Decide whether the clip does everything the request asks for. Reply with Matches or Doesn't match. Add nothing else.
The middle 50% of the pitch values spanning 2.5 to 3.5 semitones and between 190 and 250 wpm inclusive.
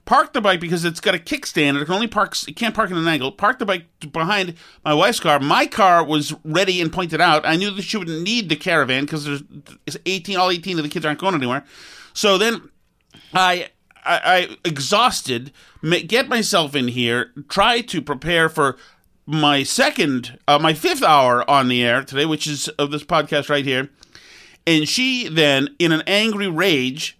Doesn't match